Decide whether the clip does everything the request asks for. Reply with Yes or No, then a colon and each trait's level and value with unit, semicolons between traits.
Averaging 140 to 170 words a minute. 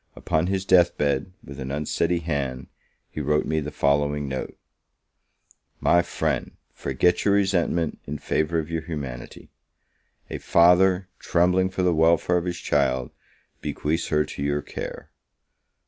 Yes: average, 145 wpm